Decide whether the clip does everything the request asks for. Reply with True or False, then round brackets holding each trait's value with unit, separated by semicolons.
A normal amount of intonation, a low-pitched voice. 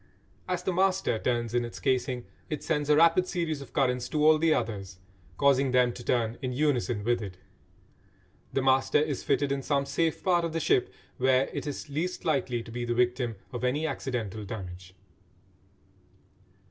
True (4.2 semitones; 130 Hz)